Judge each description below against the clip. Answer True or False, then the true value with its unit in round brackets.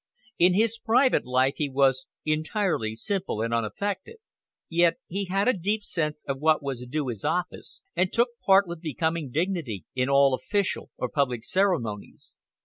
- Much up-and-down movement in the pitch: True (6.7 semitones)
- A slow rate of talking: False (160 wpm)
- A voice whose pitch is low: False (160 Hz)